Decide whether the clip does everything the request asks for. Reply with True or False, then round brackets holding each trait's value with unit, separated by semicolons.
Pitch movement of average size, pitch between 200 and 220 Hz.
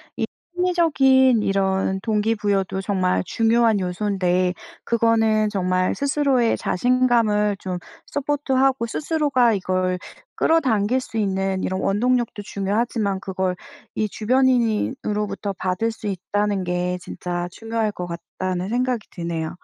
True (4.2 semitones; 210 Hz)